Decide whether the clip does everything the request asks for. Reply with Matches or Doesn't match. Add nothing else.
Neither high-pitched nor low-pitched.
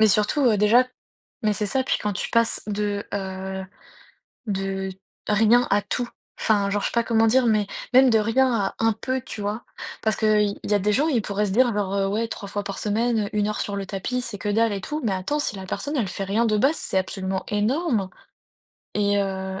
Doesn't match